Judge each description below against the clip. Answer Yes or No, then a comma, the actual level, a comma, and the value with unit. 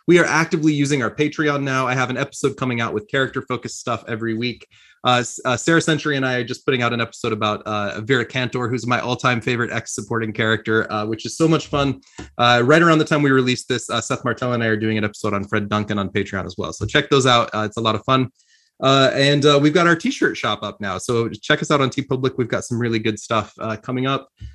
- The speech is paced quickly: Yes, fast, 260 wpm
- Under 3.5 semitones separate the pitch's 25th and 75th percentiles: No, average, 3.9 semitones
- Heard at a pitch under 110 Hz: No, low, 125 Hz